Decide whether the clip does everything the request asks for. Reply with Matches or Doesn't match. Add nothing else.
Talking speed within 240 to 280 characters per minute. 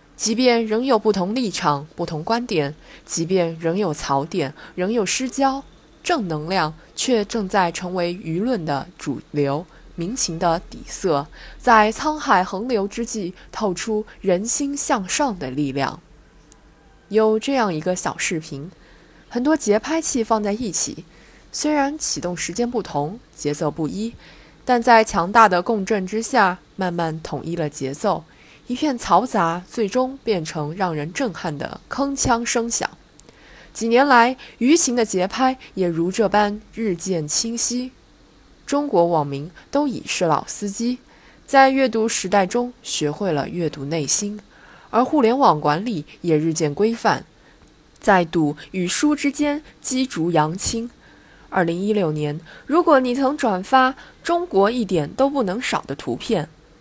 Doesn't match